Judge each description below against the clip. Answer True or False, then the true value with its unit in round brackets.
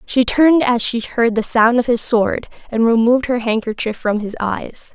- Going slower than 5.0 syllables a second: True (4.8 syllables/s)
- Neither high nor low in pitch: False (235 Hz)